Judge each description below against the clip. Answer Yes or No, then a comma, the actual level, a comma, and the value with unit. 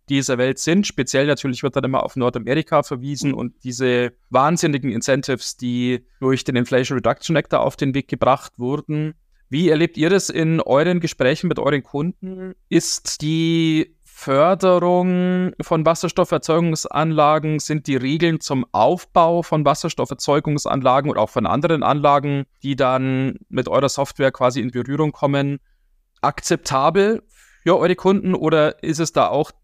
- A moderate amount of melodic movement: Yes, average, 3.7 semitones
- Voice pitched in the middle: Yes, medium, 145 Hz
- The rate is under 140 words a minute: No, average, 145 wpm